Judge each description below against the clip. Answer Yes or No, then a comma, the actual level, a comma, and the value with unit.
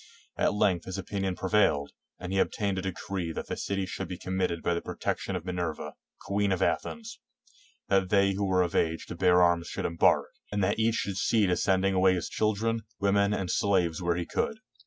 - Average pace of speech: No, fast, 210 wpm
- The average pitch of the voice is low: Yes, very low, 95 Hz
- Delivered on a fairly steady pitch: Yes, narrow, 2.1 semitones